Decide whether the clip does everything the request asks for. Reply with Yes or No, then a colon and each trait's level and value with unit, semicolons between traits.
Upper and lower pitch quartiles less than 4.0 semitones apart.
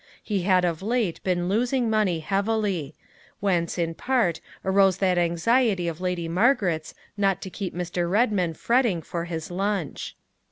Yes: average, 3.4 semitones